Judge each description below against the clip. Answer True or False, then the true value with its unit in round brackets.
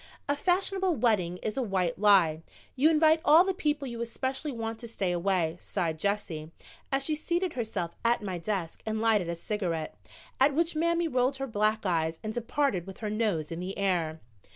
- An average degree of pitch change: False (7.5 semitones)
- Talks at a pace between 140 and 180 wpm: False (190 wpm)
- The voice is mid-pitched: False (215 Hz)